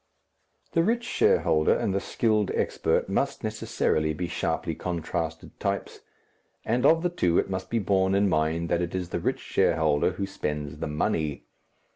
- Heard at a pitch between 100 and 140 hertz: No, very low, 90 Hz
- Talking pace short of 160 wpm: No, average, 165 wpm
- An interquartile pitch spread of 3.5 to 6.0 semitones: Yes, average, 4.0 semitones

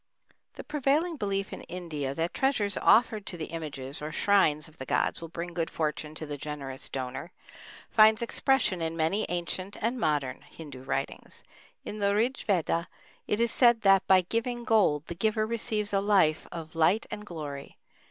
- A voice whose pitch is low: No, medium, 180 Hz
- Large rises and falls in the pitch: Yes, wide, 5.7 semitones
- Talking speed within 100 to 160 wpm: No, average, 175 wpm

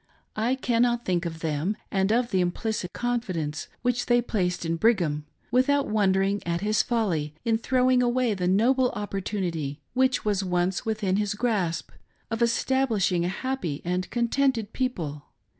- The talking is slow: No, average, 150 wpm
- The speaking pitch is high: Yes, high, 205 Hz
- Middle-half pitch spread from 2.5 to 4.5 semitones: No, average, 5.3 semitones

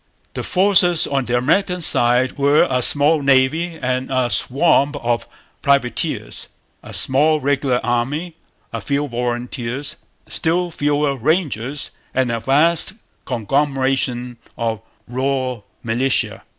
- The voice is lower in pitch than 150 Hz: Yes, low, 135 Hz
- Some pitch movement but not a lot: Yes, average, 3.3 semitones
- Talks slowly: Yes, slow, 115 wpm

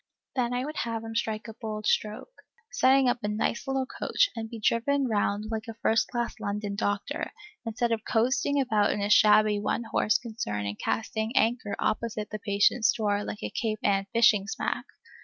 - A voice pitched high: Yes, high, 220 Hz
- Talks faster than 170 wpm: Yes, average, 190 wpm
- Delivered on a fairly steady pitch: Yes, narrow, 2.2 semitones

